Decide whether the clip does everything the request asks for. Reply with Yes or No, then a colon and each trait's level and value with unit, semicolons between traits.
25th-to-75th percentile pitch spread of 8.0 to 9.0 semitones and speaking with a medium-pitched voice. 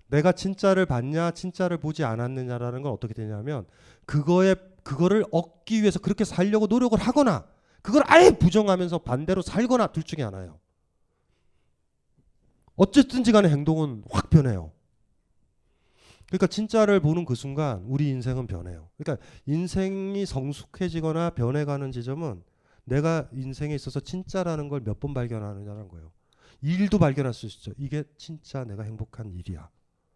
No: wide, 7.5 semitones; medium, 150 Hz